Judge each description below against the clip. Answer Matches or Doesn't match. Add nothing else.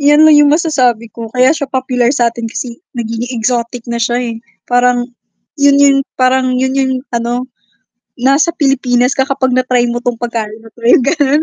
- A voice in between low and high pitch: Doesn't match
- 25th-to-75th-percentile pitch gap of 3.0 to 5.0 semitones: Doesn't match